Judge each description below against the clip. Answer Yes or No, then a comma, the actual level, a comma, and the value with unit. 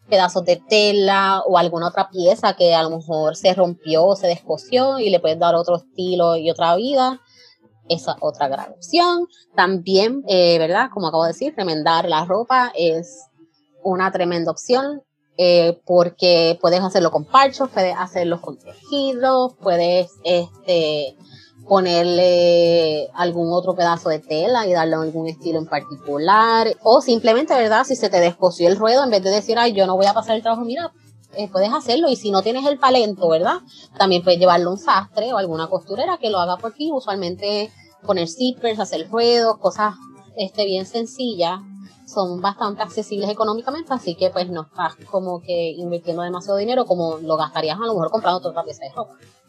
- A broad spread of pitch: No, average, 4.5 semitones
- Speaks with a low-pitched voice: No, medium, 185 Hz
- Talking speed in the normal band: Yes, average, 180 wpm